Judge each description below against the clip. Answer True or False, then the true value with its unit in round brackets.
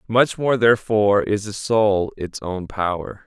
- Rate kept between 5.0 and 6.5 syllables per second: False (4.3 syllables/s)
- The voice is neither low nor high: False (105 Hz)